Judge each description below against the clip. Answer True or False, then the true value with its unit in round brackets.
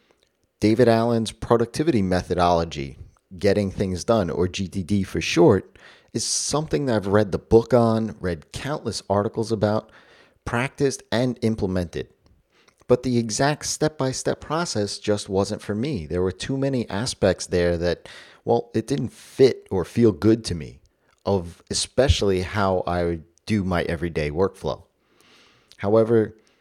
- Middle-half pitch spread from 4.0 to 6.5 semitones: True (4.3 semitones)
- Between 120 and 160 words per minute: True (140 wpm)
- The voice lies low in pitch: True (105 Hz)